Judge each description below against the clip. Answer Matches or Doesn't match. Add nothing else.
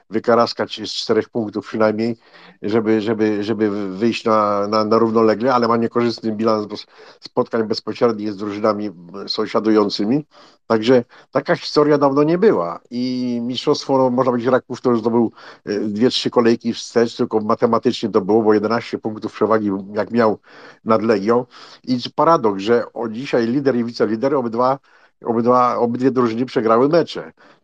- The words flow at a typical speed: Matches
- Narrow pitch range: Matches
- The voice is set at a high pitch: Doesn't match